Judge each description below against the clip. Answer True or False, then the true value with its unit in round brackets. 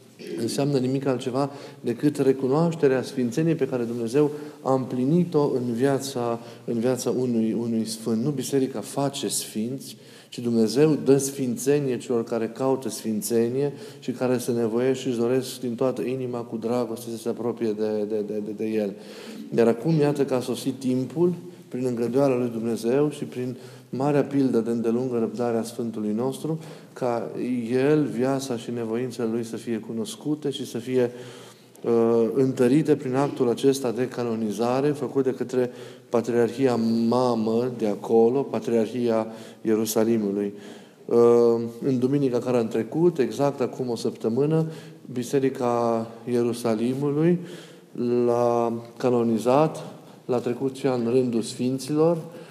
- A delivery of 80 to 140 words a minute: True (135 wpm)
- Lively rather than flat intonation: False (2.8 semitones)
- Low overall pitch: True (125 Hz)